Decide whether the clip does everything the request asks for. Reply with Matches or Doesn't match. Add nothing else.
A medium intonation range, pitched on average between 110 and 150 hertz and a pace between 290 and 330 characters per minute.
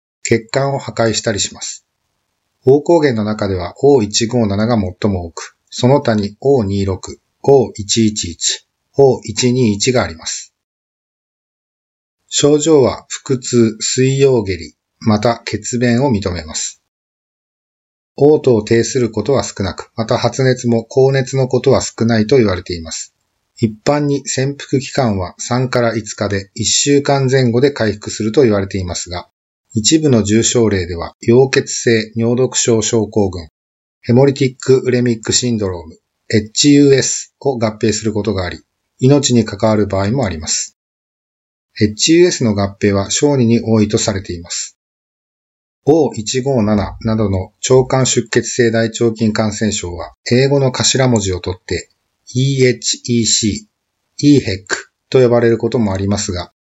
Doesn't match